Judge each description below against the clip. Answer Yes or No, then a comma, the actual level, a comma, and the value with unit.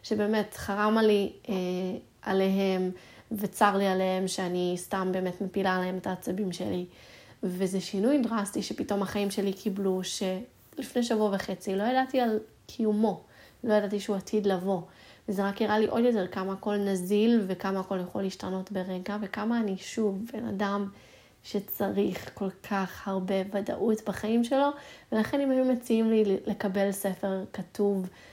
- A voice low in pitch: No, high, 200 Hz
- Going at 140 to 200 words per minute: Yes, fast, 150 wpm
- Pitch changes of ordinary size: No, narrow, 2.2 semitones